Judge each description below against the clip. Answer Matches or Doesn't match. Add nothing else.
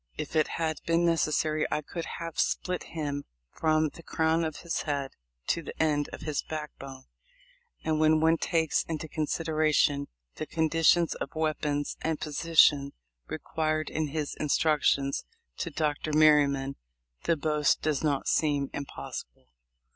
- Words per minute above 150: Doesn't match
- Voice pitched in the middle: Matches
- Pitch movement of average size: Doesn't match